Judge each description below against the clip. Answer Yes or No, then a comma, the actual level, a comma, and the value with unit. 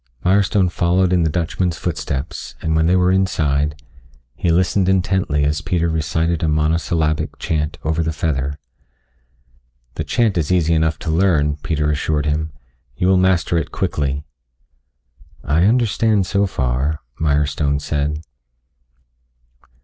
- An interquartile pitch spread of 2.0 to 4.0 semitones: Yes, average, 3.3 semitones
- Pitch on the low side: Yes, very low, 80 Hz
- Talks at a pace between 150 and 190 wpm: No, slow, 135 wpm